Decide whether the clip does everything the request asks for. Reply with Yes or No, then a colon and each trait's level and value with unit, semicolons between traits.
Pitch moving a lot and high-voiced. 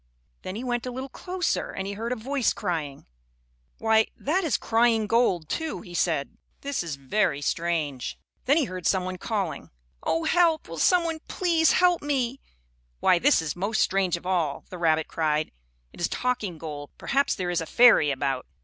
Yes: wide, 7.8 semitones; high, 195 Hz